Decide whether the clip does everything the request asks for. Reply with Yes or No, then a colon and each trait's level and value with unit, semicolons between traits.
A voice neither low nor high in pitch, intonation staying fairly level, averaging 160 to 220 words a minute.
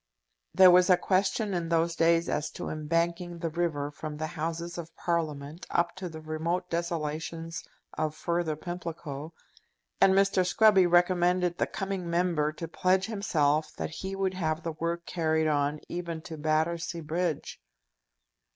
No: medium, 170 Hz; narrow, 2.1 semitones; average, 150 wpm